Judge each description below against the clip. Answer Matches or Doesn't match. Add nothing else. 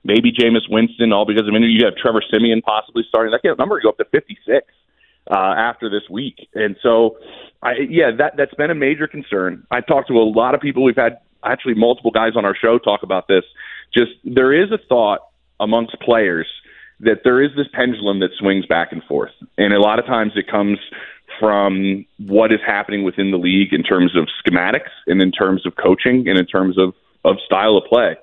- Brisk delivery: Matches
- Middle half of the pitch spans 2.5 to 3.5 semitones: Doesn't match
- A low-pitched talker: Matches